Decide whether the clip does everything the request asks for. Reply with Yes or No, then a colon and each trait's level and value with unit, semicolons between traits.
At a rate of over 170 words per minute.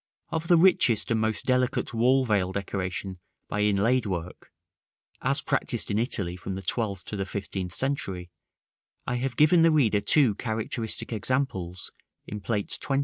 No: average, 155 wpm